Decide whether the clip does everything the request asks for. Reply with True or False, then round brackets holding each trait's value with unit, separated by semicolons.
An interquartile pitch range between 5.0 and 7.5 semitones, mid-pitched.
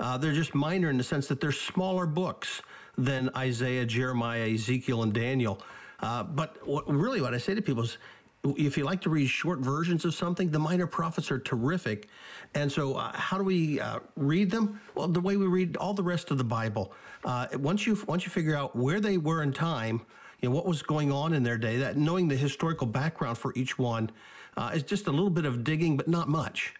True (5.6 semitones; 150 Hz)